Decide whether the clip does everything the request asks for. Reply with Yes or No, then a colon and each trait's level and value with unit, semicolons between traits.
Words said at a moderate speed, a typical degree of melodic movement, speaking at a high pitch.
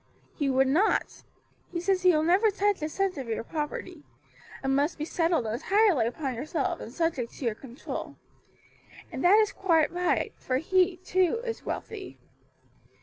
No: average, 165 wpm; wide, 5.7 semitones; very high, 330 Hz